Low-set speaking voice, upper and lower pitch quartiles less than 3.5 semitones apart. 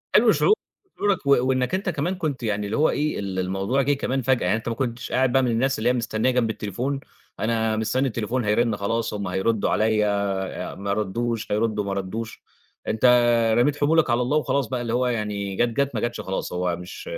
No: low, 115 Hz; average, 3.9 semitones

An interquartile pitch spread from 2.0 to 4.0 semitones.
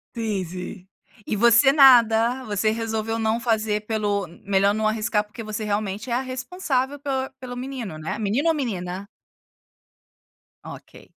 Yes: average, 3.5 semitones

